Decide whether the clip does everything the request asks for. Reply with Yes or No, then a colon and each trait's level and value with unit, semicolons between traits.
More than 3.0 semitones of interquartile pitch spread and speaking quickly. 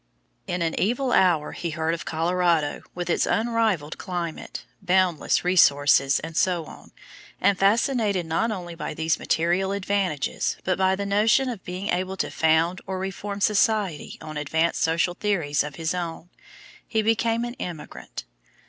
No: average, 3.6 semitones; average, 150 wpm